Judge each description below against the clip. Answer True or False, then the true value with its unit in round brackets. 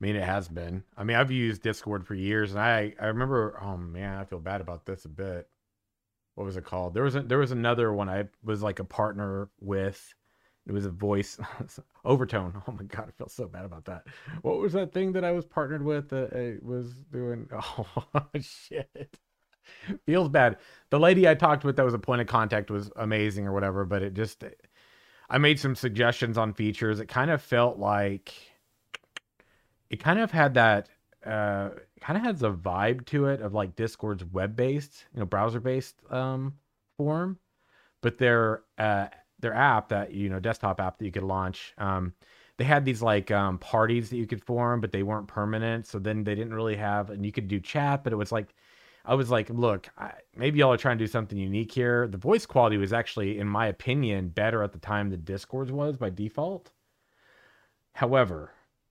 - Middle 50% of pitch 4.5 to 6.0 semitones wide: False (3.9 semitones)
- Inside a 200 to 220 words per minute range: True (205 wpm)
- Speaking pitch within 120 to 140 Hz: False (110 Hz)